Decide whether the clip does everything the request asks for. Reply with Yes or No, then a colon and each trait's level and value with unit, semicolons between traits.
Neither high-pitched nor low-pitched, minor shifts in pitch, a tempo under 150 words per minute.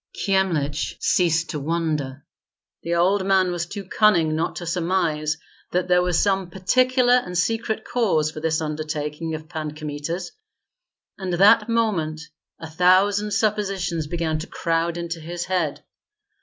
No: medium, 175 Hz; average, 3.4 semitones; average, 140 wpm